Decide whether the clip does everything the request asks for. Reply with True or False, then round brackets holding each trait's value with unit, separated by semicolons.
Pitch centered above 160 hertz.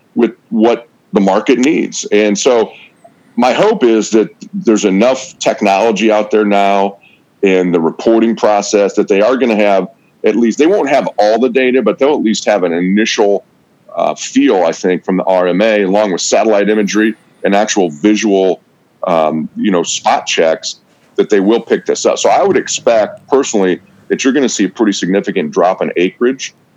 False (105 Hz)